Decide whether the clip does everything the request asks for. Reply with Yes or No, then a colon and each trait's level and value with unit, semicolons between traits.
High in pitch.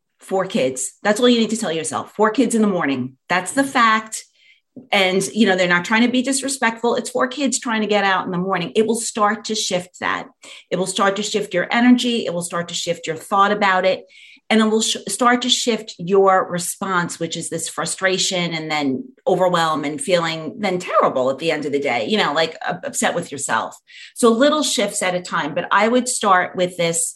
Yes: high, 195 Hz